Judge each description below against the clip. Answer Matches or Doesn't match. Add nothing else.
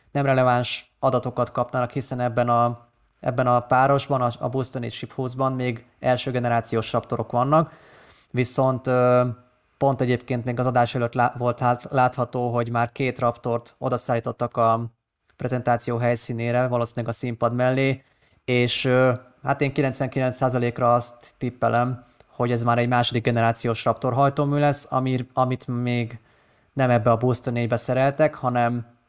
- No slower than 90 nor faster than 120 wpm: Doesn't match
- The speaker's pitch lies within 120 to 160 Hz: Matches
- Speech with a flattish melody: Matches